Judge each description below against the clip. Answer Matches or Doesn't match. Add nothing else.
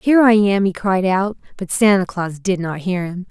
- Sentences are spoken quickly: Matches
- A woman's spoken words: Matches